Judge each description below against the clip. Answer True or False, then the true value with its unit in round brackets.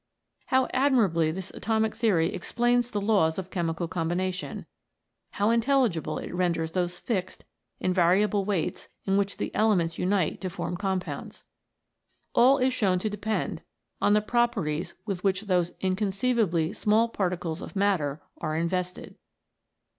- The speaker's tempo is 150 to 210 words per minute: False (140 wpm)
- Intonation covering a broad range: False (3.8 semitones)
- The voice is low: False (190 Hz)